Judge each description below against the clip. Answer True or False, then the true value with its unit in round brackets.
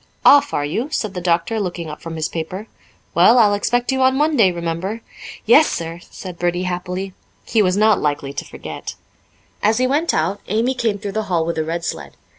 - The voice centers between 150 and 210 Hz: True (190 Hz)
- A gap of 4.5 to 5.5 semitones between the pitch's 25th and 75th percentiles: True (5.2 semitones)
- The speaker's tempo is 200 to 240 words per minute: True (205 wpm)